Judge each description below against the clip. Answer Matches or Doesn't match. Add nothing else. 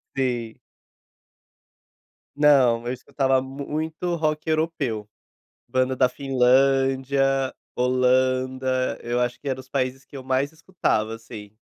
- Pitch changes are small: Matches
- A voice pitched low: Matches